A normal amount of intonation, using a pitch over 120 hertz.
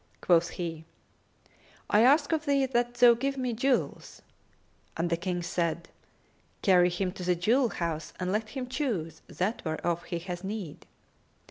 No: wide, 6.2 semitones; high, 190 Hz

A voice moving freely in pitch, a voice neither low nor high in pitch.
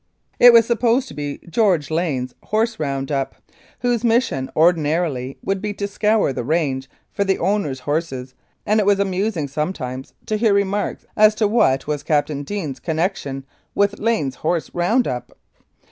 Yes: wide, 6.8 semitones; medium, 175 Hz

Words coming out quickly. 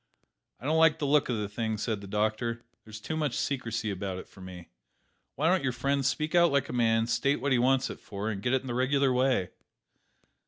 Yes: fast, 235 wpm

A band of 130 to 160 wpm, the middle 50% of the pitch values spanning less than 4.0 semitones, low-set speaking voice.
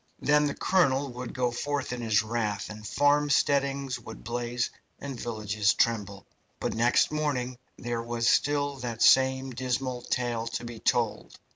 Yes: average, 150 wpm; average, 2.9 semitones; low, 125 Hz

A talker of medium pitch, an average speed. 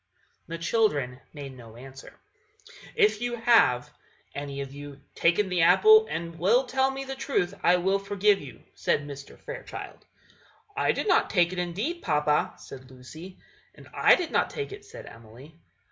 Yes: medium, 175 Hz; average, 165 wpm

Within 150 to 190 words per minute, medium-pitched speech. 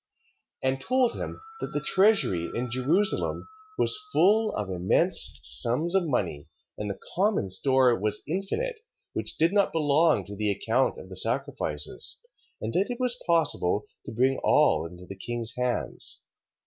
No: average, 155 wpm; low, 130 Hz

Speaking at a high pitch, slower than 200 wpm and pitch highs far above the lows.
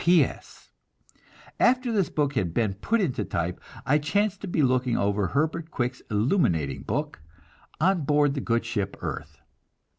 No: medium, 140 Hz; average, 155 wpm; wide, 8.1 semitones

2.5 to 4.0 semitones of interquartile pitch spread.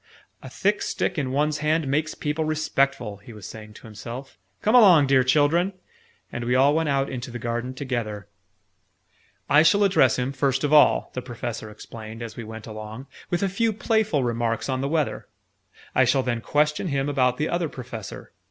No: average, 4.4 semitones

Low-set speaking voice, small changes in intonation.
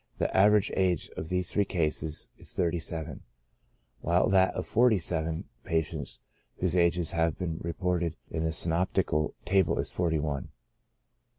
Yes: very low, 85 Hz; narrow, 2.2 semitones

